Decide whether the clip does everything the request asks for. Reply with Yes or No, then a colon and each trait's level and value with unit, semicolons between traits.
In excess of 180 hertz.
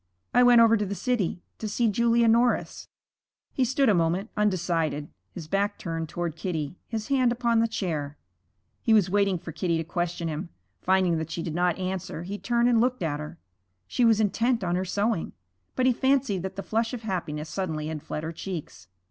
Yes: high, 190 Hz